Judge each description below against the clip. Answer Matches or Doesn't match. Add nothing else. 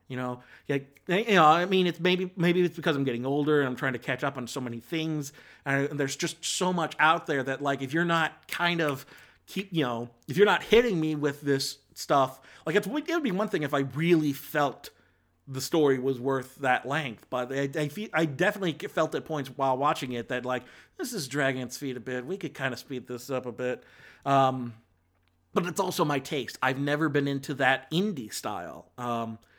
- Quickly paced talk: Matches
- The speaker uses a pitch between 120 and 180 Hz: Matches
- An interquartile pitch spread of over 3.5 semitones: Matches